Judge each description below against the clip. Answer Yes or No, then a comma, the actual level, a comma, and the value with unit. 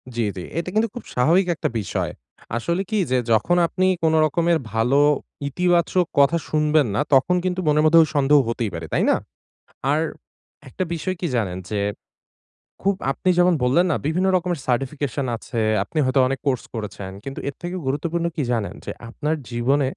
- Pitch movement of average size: No, wide, 5.7 semitones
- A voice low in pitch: No, medium, 150 Hz